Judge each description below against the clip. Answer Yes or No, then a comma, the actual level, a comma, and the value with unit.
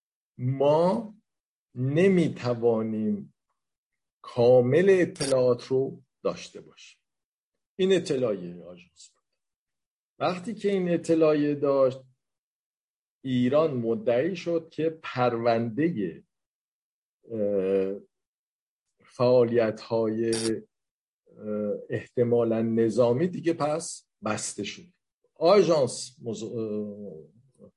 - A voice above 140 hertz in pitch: No, low, 125 Hz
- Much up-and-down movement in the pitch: Yes, wide, 6.1 semitones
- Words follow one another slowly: Yes, slow, 65 wpm